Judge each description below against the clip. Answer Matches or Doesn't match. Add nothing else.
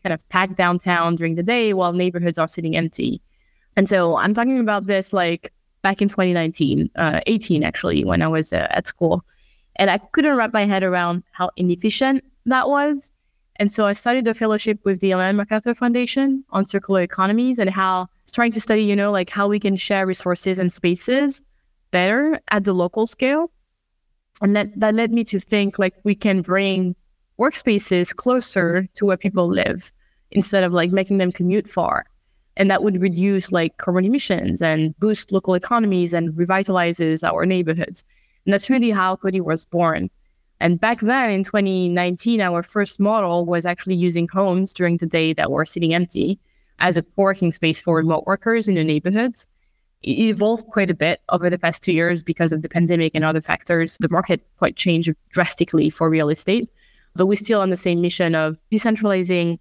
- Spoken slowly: Doesn't match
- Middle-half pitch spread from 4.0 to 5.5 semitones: Doesn't match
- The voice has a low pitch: Doesn't match